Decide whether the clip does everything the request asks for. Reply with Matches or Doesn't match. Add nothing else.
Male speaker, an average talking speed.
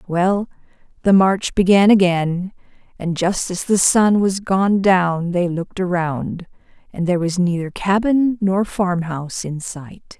Doesn't match